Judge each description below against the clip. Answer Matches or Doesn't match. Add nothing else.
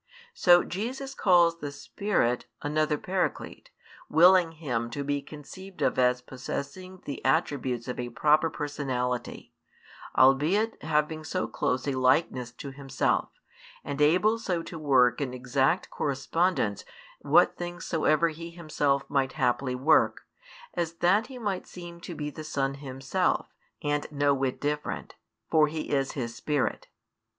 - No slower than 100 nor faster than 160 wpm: Matches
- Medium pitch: Matches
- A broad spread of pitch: Doesn't match